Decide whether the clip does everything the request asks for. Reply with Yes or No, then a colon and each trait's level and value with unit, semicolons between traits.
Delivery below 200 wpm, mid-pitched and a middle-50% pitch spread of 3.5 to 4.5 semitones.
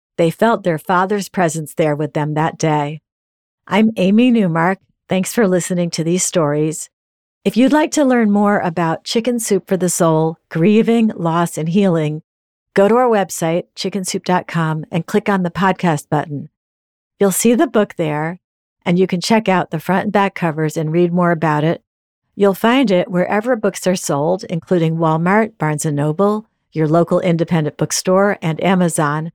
Yes: average, 170 wpm; medium, 180 Hz; average, 3.9 semitones